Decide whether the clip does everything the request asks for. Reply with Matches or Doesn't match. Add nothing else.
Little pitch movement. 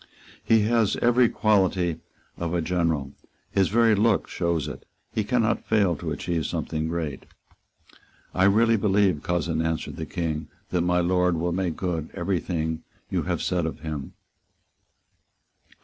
Doesn't match